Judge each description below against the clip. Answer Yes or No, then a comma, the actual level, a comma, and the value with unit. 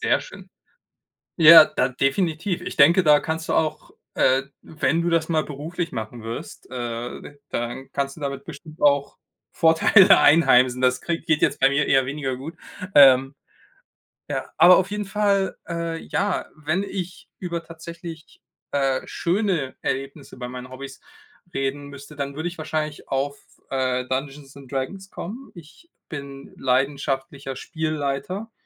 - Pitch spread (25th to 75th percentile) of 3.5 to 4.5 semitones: Yes, average, 3.8 semitones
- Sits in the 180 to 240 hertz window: No, medium, 145 Hz